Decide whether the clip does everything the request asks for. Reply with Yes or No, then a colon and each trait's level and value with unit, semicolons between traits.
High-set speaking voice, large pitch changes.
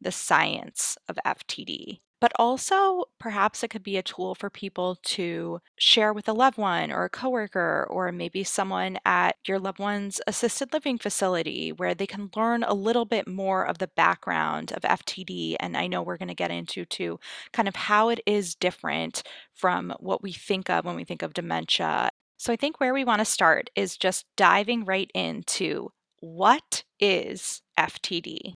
No: high, 200 Hz; average, 4.3 semitones